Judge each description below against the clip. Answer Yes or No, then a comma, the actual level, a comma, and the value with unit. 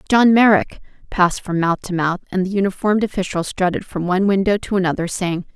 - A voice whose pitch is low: No, high, 190 Hz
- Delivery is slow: No, fast, 205 wpm